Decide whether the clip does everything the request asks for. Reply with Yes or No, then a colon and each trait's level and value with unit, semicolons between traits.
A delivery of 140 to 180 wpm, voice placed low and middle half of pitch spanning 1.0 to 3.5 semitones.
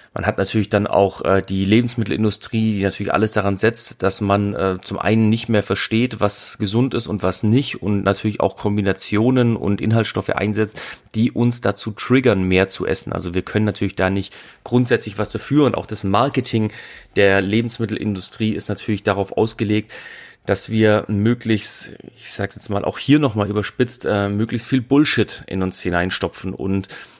Yes: average, 175 wpm; low, 105 Hz; narrow, 2.4 semitones